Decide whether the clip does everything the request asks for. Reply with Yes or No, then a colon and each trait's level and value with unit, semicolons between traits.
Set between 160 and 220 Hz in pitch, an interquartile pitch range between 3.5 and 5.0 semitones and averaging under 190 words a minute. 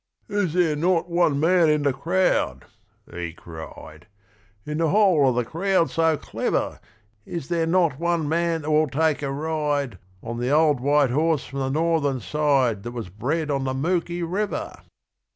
No: medium, 150 Hz; average, 3.8 semitones; average, 170 wpm